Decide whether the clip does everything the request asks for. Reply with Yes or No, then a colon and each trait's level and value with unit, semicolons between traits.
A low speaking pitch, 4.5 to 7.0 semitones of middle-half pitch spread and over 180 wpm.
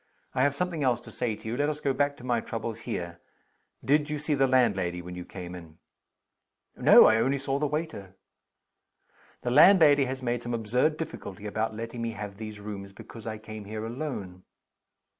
Yes: low, 115 Hz; average, 5.2 semitones; average, 195 wpm